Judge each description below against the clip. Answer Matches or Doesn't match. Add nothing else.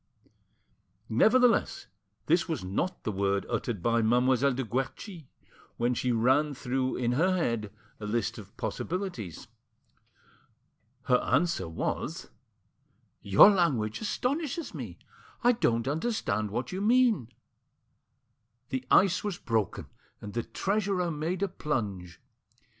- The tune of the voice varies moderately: Doesn't match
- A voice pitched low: Matches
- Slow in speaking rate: Matches